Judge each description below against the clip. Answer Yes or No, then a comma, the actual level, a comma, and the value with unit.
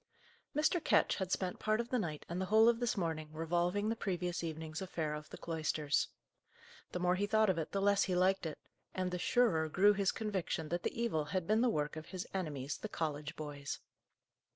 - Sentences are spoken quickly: Yes, fast, 215 wpm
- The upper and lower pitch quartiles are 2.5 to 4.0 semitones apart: No, average, 4.5 semitones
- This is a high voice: No, medium, 180 Hz